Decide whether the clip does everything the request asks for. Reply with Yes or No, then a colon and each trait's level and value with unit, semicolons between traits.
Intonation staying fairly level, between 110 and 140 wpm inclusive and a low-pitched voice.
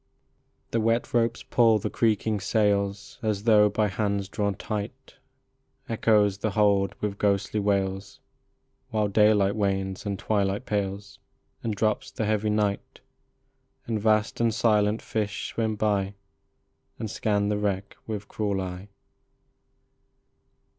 Yes: narrow, 1.5 semitones; slow, 135 wpm; low, 105 Hz